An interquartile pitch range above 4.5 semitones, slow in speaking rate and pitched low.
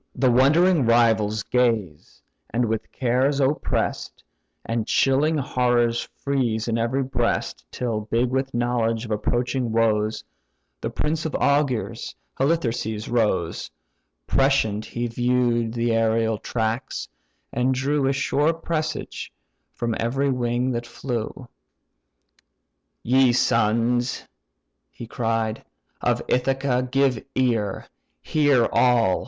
No: average, 2.7 semitones; slow, 110 wpm; low, 120 Hz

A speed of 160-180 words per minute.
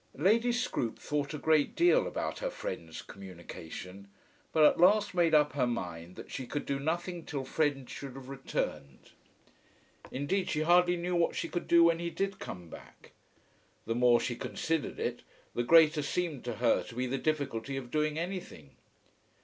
Yes: average, 175 wpm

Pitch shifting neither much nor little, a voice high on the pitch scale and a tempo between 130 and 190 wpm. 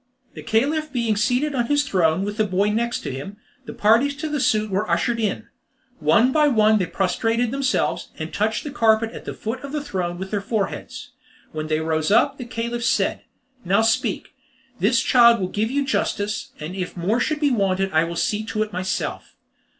No: average, 4.5 semitones; high, 220 Hz; average, 200 wpm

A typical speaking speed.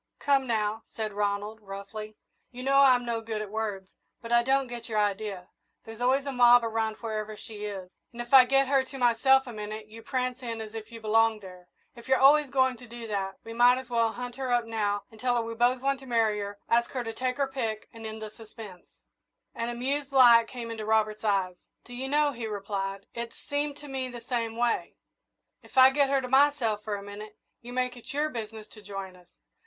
No: fast, 225 wpm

